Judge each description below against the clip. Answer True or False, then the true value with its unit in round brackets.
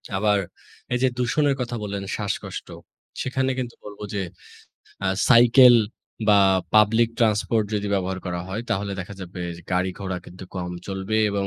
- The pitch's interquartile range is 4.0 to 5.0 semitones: False (3.6 semitones)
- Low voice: True (105 Hz)